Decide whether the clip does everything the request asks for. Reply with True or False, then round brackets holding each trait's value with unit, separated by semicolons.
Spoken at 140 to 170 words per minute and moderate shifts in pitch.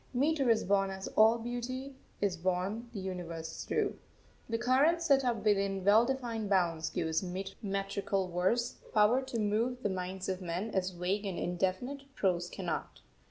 True (160 wpm; 4.4 semitones)